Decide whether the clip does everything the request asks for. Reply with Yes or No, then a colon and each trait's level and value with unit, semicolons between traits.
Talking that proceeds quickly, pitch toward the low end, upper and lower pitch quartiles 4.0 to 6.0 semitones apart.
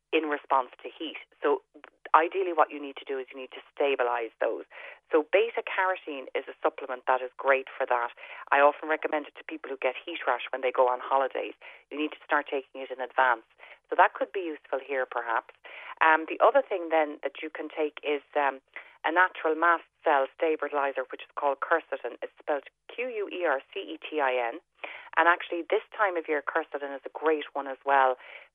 No: fast, 215 wpm; medium, 150 Hz; average, 4.3 semitones